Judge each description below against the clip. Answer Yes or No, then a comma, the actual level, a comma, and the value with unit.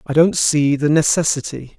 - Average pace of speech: Yes, average, 170 wpm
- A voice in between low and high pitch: Yes, medium, 150 Hz